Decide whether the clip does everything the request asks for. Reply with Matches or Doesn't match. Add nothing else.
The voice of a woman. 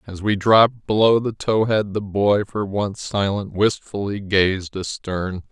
Doesn't match